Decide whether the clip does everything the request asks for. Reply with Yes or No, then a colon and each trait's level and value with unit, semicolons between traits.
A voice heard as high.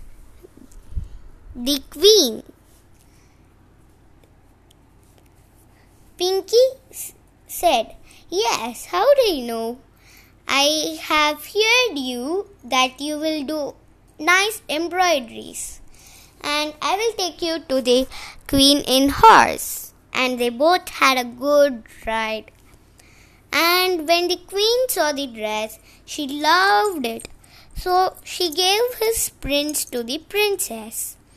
Yes: very high, 290 Hz